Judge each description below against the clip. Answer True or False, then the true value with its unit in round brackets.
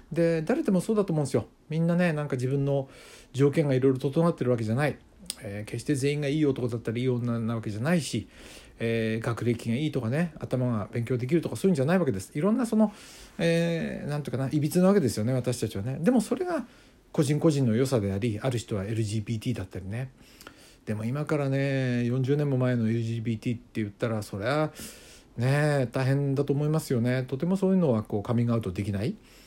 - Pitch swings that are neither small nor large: True (4.9 semitones)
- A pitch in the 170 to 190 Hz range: False (130 Hz)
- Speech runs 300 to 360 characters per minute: False (430 characters per minute)